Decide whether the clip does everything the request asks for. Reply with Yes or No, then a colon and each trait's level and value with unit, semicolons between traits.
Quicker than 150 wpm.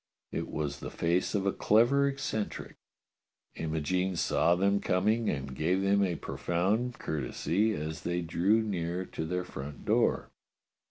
No: average, 145 wpm